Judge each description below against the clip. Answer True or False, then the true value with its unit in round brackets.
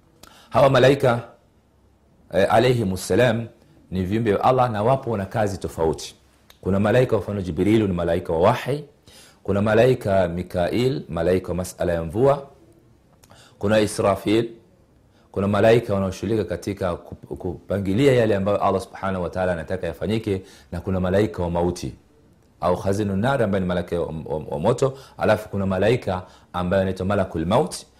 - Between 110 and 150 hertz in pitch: False (100 Hz)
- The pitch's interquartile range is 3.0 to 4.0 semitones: True (3.6 semitones)